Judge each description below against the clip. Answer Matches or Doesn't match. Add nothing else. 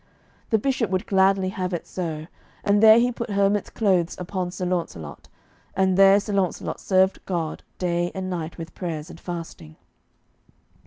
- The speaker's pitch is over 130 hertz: Matches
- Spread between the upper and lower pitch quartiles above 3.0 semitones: Doesn't match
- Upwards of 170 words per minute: Doesn't match